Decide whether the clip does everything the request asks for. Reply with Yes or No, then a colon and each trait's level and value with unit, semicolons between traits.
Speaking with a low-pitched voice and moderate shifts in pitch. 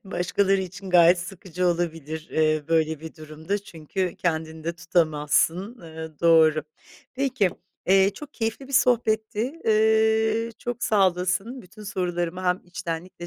No: medium, 180 Hz; average, 4.7 semitones